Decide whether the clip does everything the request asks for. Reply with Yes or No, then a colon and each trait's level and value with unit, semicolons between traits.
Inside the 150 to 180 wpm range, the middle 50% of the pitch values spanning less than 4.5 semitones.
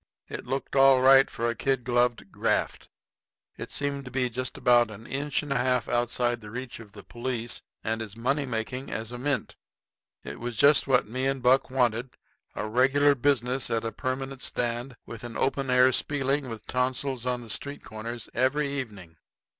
No: average, 190 wpm; narrow, 2.4 semitones